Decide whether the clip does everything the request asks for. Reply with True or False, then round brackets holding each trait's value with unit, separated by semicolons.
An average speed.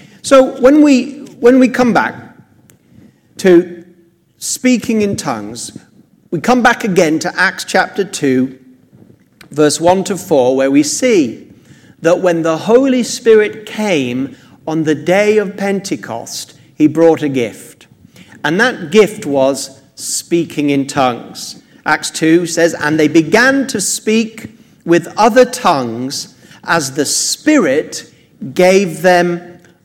False (130 wpm)